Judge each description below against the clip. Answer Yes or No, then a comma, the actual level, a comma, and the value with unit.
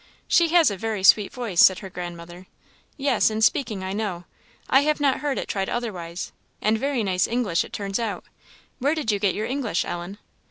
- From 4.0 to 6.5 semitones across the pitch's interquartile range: Yes, average, 5.2 semitones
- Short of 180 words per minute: No, average, 200 wpm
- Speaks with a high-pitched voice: Yes, high, 215 Hz